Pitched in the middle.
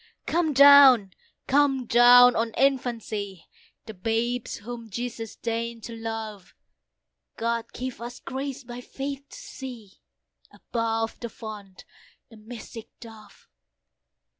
No: high, 235 Hz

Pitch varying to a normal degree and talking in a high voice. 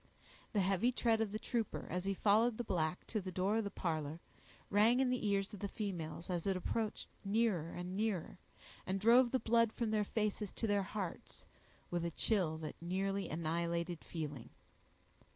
Yes: average, 4.2 semitones; high, 195 Hz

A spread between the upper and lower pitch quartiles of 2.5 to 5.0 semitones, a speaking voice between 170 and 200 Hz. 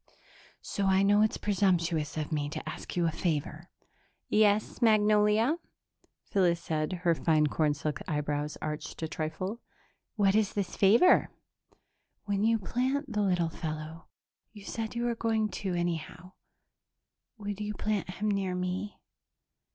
Yes: average, 4.7 semitones; high, 190 Hz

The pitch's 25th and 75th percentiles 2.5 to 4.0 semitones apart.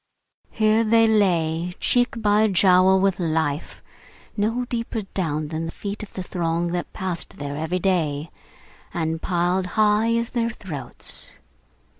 No: average, 4.7 semitones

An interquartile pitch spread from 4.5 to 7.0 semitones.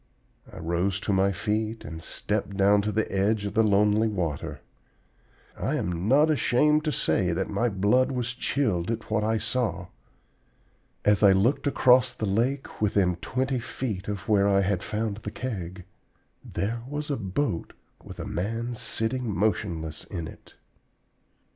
No: average, 3.8 semitones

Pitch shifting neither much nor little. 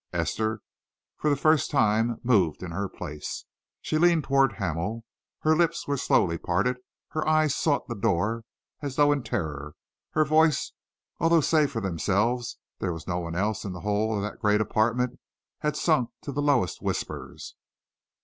No: wide, 6.8 semitones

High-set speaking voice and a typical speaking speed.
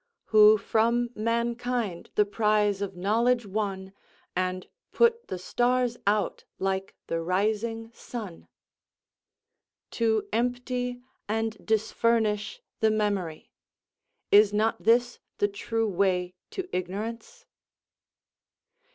No: high, 215 Hz; slow, 100 wpm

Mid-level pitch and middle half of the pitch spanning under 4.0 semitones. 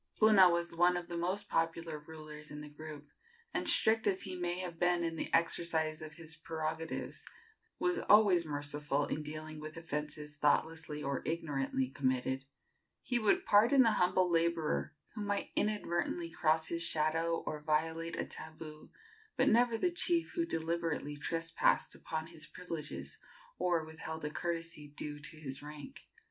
Yes: medium, 165 Hz; narrow, 2.4 semitones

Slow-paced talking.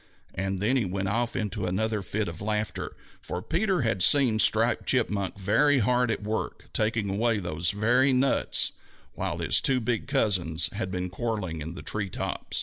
No: average, 175 wpm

